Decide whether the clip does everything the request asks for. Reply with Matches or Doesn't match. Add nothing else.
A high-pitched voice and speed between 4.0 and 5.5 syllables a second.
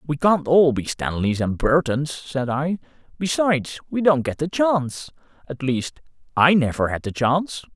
Doesn't match